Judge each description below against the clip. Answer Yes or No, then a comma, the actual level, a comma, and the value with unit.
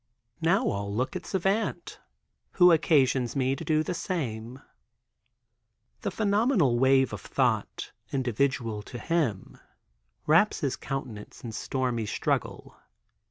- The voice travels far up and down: Yes, wide, 6.2 semitones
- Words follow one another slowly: Yes, slow, 115 wpm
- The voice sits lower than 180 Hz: Yes, low, 135 Hz